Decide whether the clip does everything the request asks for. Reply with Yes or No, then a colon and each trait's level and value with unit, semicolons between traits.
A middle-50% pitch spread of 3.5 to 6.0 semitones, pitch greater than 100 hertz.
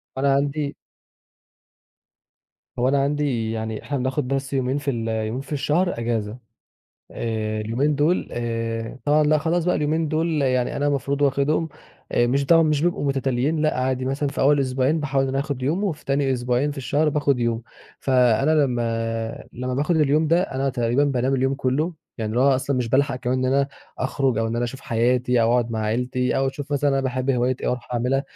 No: average, 2.9 semitones; low, 135 Hz